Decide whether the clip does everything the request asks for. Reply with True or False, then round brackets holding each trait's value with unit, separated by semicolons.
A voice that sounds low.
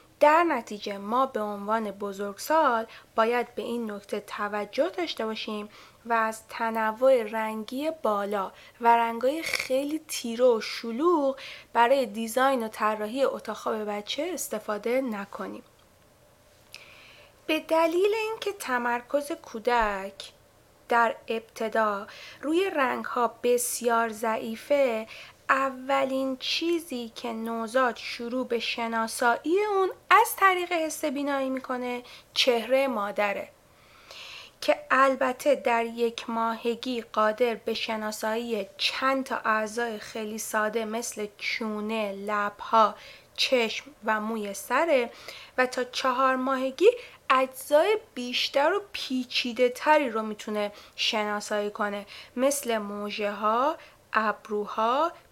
False (235 Hz)